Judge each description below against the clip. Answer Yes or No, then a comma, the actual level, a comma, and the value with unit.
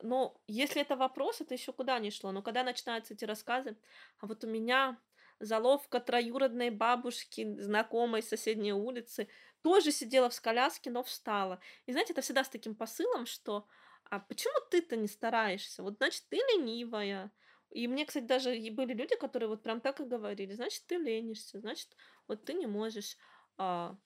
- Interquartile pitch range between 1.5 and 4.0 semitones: Yes, average, 3.5 semitones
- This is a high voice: Yes, high, 240 Hz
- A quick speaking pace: Yes, fast, 170 wpm